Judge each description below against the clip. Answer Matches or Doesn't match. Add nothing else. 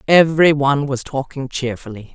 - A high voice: Doesn't match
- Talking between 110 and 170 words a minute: Matches